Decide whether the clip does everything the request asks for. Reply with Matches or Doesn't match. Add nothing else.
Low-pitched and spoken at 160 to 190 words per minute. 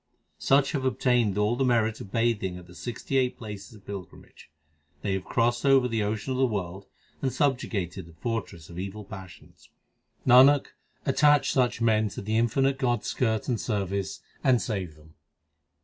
Matches